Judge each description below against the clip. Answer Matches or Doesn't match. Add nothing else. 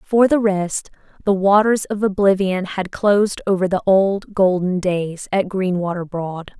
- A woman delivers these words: Matches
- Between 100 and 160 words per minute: Matches